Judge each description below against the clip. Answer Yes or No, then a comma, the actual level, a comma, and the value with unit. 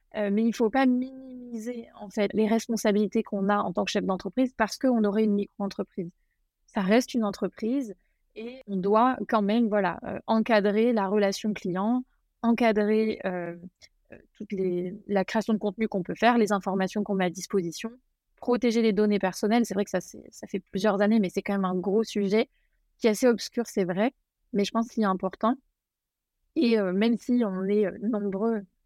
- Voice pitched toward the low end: No, high, 215 Hz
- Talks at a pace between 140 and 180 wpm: No, average, 200 wpm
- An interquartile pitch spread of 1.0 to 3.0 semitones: Yes, narrow, 2.6 semitones